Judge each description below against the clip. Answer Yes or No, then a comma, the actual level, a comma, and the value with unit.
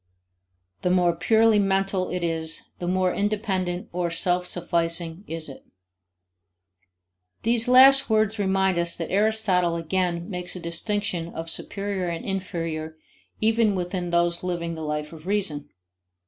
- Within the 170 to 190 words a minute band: No, slow, 135 wpm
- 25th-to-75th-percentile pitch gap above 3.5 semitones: No, average, 2.9 semitones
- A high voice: No, medium, 180 Hz